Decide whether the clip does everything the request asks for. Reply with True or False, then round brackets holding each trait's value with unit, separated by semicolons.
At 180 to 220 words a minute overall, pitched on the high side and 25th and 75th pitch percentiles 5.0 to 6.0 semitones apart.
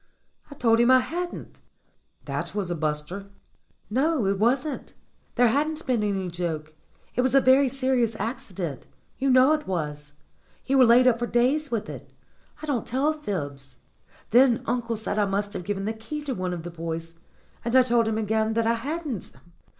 True (185 wpm; 230 Hz; 5.3 semitones)